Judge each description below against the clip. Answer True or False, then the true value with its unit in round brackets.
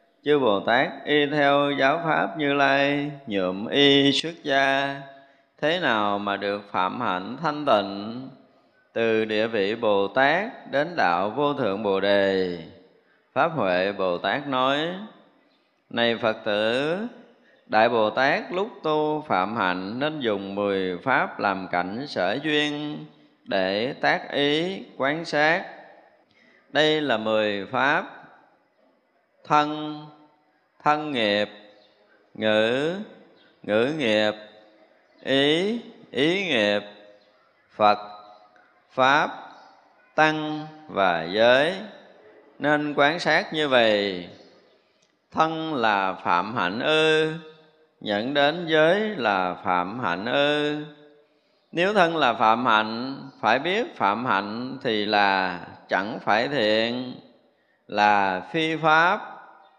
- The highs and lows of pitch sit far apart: True (6.6 semitones)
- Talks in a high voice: False (135 Hz)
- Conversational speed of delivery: False (110 wpm)